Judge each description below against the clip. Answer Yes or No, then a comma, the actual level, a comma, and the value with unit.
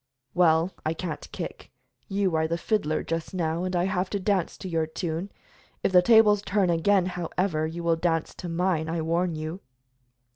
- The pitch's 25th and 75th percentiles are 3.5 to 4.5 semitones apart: No, narrow, 2.5 semitones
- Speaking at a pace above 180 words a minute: Yes, average, 190 wpm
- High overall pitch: No, medium, 175 Hz